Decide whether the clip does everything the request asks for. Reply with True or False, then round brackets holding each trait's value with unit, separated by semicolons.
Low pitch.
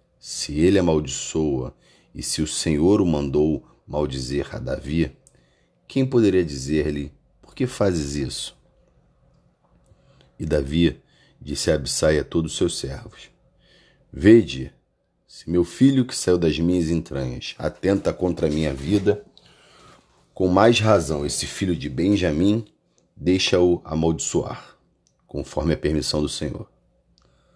True (80 Hz)